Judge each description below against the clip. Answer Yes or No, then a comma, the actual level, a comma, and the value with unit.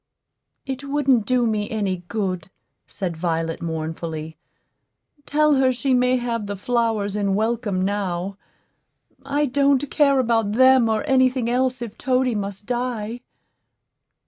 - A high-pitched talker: Yes, high, 230 Hz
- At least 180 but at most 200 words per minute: No, slow, 135 wpm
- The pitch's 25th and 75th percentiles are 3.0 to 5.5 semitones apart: Yes, average, 4.5 semitones